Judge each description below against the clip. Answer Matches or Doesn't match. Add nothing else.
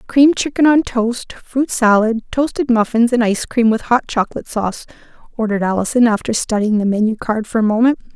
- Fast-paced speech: Doesn't match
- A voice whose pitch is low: Doesn't match